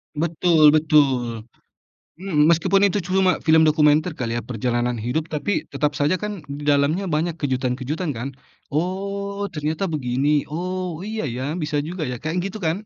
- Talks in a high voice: No, medium, 155 Hz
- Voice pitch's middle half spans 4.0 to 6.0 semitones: Yes, average, 4.4 semitones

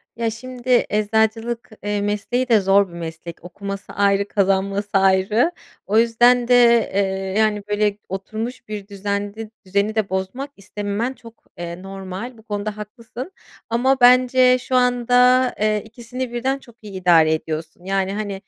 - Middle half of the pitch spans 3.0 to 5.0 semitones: Yes, average, 3.6 semitones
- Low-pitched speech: No, high, 210 Hz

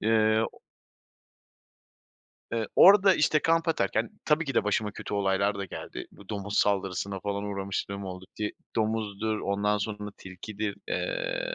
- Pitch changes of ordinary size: No, narrow, 2.1 semitones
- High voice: No, low, 105 Hz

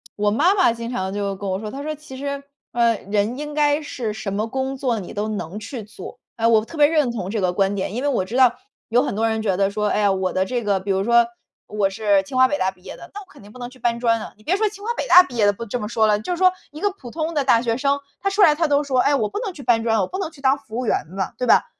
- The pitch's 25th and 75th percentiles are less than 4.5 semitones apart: No, wide, 5.6 semitones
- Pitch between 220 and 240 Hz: Yes, high, 235 Hz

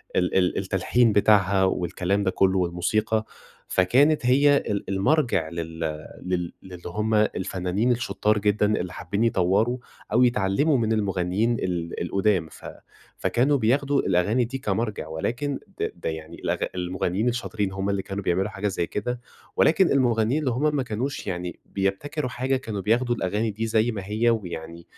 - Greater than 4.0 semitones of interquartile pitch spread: Yes, average, 4.6 semitones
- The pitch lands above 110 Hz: No, low, 105 Hz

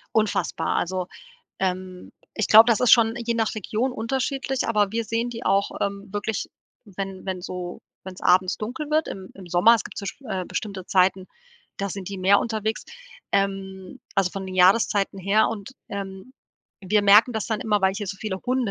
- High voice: Yes, high, 200 Hz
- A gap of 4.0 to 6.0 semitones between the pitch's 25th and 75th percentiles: No, average, 2.9 semitones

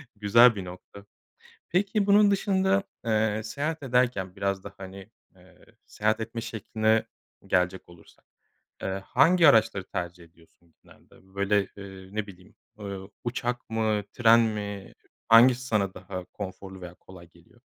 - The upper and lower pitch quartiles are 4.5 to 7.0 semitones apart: No, average, 3.8 semitones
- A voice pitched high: No, low, 105 Hz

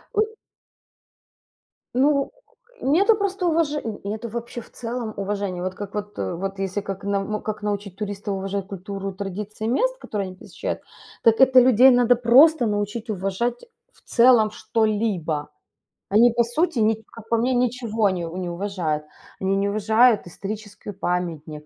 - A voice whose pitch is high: Yes, high, 210 Hz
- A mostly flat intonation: No, average, 3.7 semitones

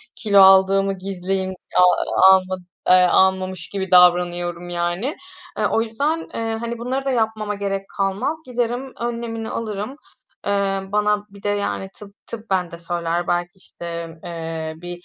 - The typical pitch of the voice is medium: No, high, 195 Hz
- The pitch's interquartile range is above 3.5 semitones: Yes, average, 3.9 semitones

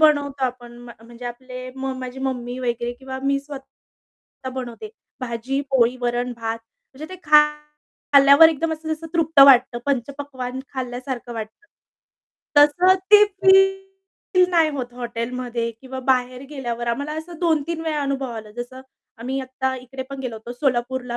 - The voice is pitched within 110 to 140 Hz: No, very high, 260 Hz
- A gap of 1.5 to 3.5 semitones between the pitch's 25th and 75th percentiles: Yes, average, 3.2 semitones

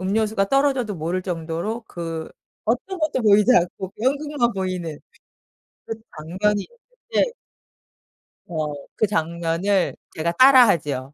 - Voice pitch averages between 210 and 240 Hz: No, high, 195 Hz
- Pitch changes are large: Yes, wide, 6.7 semitones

